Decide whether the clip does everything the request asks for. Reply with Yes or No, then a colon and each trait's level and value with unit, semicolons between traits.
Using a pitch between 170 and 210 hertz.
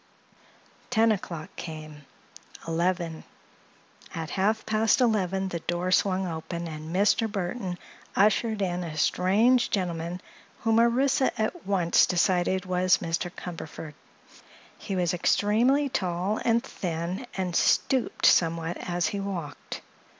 Yes: medium, 185 Hz